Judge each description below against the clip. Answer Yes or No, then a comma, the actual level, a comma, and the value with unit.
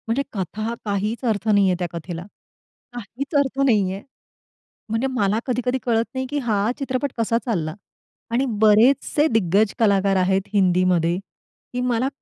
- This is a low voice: No, high, 215 Hz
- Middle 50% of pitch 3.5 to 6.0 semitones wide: Yes, average, 4.5 semitones